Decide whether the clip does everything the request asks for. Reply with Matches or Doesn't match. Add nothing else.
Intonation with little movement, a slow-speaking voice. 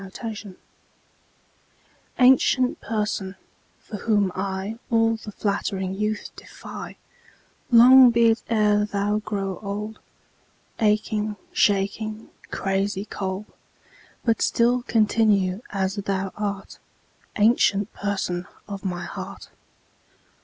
Matches